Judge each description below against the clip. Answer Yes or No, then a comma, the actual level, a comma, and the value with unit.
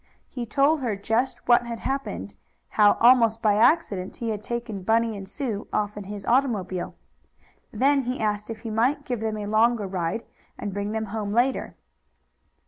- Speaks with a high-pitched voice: Yes, high, 225 Hz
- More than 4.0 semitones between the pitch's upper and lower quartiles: No, average, 2.8 semitones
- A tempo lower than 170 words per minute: No, average, 175 wpm